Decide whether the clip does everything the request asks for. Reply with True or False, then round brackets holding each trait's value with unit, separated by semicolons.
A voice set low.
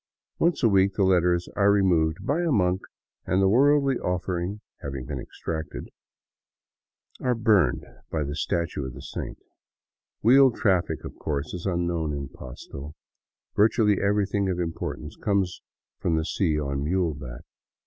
True (90 Hz)